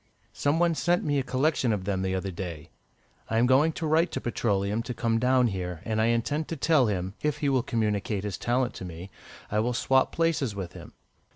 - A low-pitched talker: Yes, low, 115 Hz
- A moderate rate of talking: No, fast, 220 wpm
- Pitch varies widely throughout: Yes, wide, 6.1 semitones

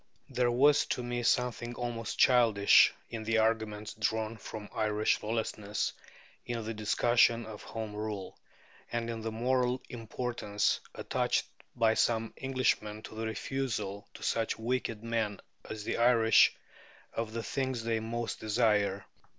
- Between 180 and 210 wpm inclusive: No, average, 140 wpm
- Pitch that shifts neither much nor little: No, narrow, 1.8 semitones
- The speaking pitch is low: Yes, low, 115 Hz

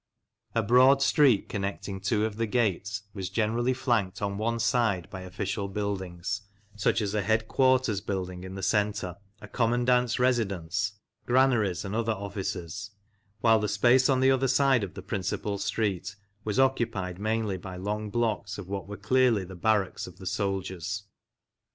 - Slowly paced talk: No, average, 160 wpm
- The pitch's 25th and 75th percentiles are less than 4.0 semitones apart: Yes, average, 3.3 semitones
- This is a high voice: No, low, 105 Hz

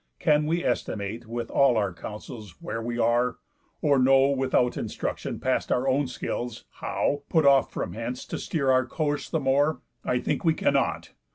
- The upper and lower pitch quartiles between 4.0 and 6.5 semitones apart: No, average, 3.2 semitones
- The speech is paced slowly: No, average, 175 wpm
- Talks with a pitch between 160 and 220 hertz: No, low, 130 Hz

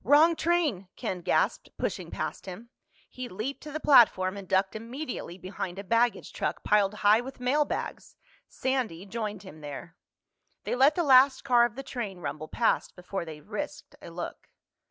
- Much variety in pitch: Yes, wide, 5.9 semitones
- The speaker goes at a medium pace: Yes, average, 170 wpm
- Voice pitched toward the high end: Yes, high, 225 Hz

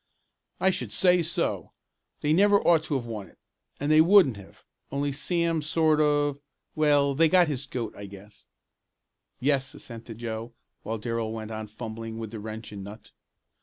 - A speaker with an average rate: Yes, average, 170 wpm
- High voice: No, low, 135 Hz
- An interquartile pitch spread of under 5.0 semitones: No, wide, 5.6 semitones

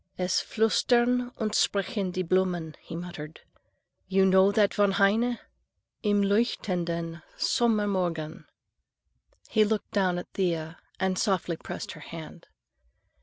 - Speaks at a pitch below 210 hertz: Yes, high, 190 Hz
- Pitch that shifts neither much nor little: Yes, average, 3.5 semitones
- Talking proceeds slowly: Yes, slow, 120 wpm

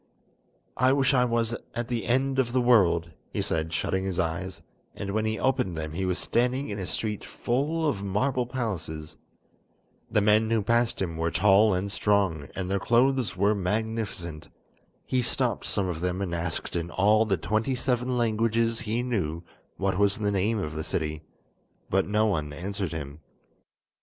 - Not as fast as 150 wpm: No, average, 175 wpm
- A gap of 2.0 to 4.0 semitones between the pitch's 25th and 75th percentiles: No, average, 4.8 semitones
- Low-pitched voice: Yes, low, 105 Hz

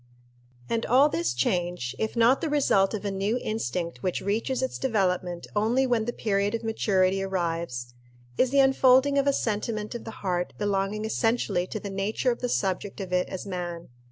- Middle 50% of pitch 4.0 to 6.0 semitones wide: Yes, average, 4.6 semitones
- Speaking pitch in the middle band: No, high, 205 Hz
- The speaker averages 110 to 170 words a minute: No, average, 185 wpm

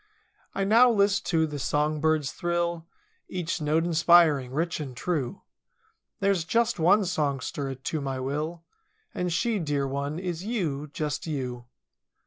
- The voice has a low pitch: No, medium, 160 Hz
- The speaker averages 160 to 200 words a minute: No, average, 140 wpm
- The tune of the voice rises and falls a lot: No, average, 3.7 semitones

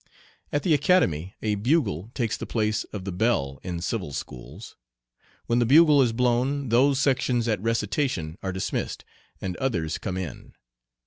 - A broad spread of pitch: Yes, wide, 6.1 semitones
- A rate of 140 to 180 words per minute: Yes, average, 155 wpm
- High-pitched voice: No, low, 115 Hz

